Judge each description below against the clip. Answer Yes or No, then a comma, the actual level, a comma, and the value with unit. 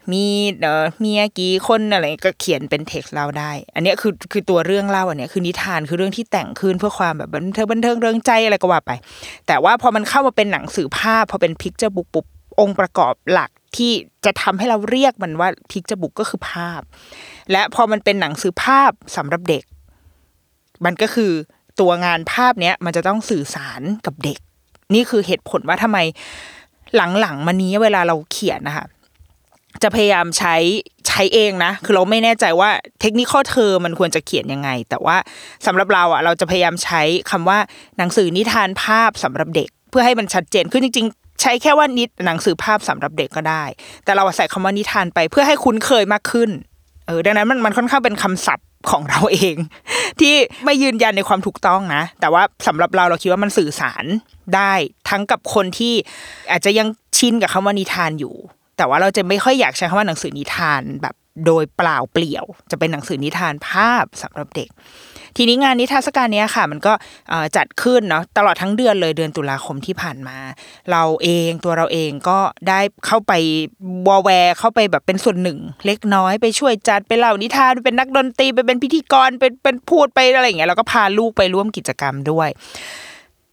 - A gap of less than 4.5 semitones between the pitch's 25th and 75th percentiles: No, average, 4.9 semitones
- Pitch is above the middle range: Yes, high, 195 Hz